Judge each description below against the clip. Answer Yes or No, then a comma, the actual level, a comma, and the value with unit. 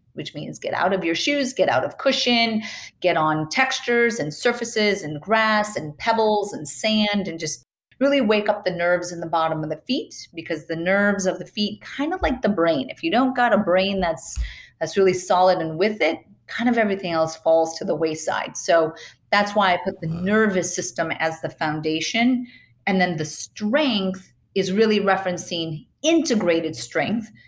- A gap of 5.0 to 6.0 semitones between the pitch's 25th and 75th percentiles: Yes, average, 5.3 semitones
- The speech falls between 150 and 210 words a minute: Yes, average, 190 wpm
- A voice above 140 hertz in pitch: Yes, high, 190 Hz